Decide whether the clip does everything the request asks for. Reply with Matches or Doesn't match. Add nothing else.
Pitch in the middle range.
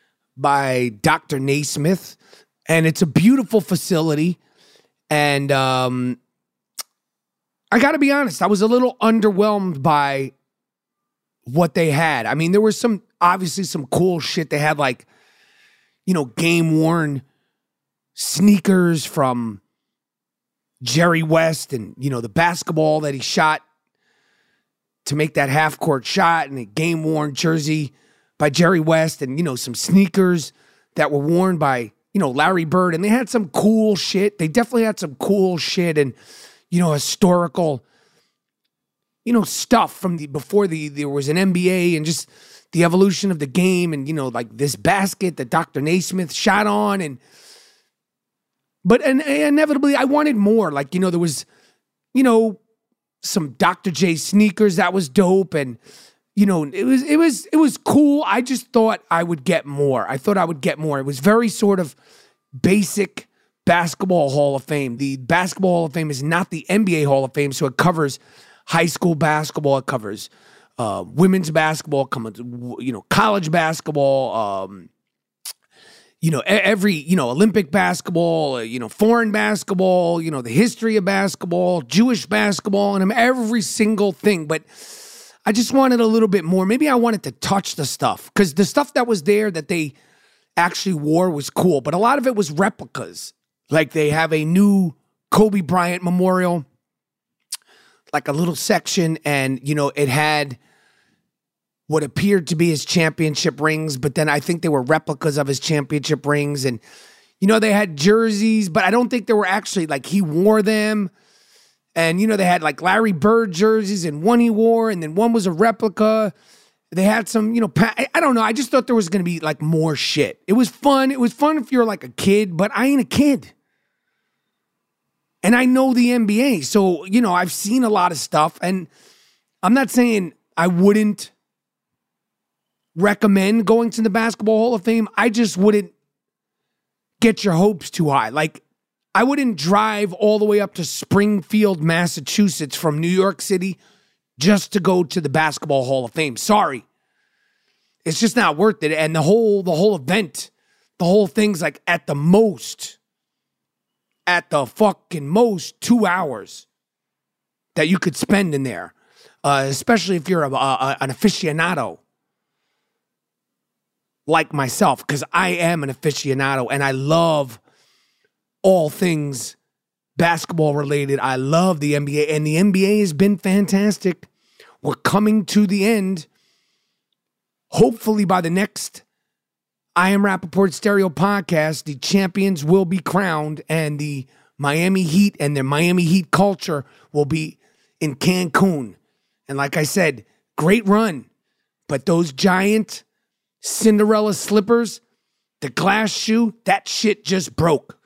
Matches